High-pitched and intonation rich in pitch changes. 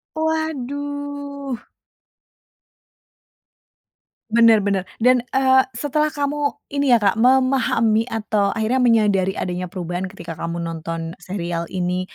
Yes: high, 225 Hz; wide, 7.0 semitones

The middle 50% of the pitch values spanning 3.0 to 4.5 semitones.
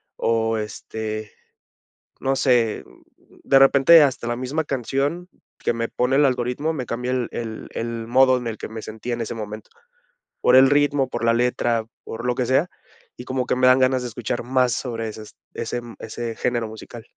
No: narrow, 2.5 semitones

